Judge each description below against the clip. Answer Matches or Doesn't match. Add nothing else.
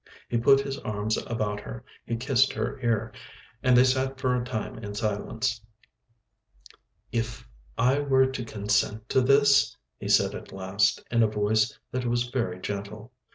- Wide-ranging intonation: Doesn't match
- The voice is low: Matches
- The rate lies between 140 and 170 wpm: Matches